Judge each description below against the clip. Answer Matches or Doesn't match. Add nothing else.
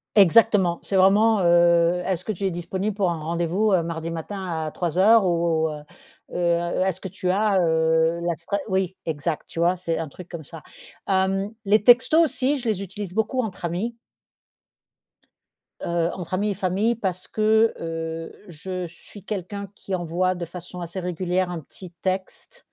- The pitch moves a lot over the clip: Doesn't match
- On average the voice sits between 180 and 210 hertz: Matches